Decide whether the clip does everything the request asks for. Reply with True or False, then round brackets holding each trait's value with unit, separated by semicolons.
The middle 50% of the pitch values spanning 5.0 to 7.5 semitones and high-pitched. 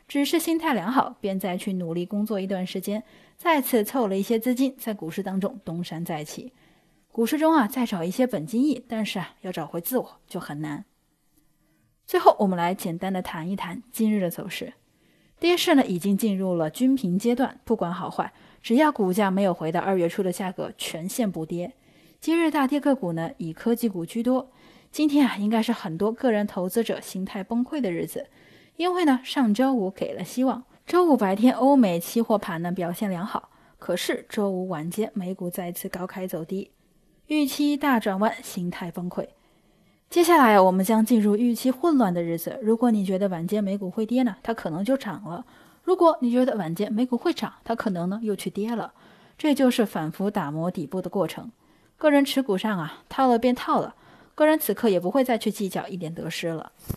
True (5.6 semitones; 210 Hz)